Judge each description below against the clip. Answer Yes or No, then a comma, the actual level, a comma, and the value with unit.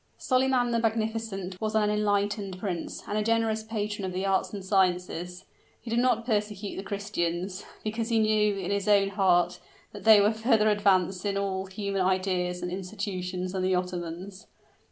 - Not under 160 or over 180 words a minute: Yes, average, 175 wpm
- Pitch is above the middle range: Yes, high, 200 Hz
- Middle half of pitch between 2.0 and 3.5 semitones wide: Yes, narrow, 2.6 semitones